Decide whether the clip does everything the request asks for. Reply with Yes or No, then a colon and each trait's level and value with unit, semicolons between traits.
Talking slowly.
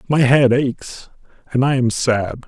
No: average, 170 wpm